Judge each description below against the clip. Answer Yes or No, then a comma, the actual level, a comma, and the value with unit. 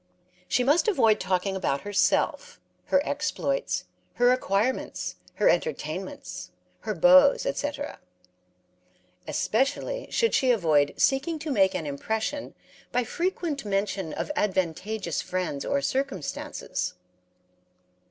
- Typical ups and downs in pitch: No, wide, 7.2 semitones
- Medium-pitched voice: No, very high, 250 Hz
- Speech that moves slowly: Yes, slow, 105 wpm